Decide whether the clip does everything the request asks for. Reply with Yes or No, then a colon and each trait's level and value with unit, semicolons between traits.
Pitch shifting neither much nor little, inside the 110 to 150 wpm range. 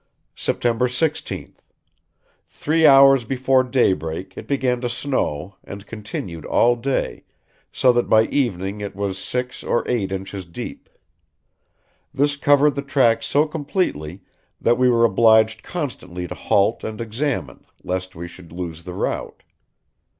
No: wide, 5.9 semitones; slow, 135 wpm